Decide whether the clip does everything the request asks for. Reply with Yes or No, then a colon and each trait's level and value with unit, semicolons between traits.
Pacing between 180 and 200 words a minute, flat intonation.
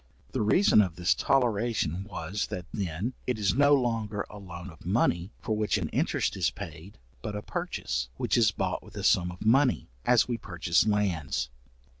No: average, 185 wpm; average, 4.5 semitones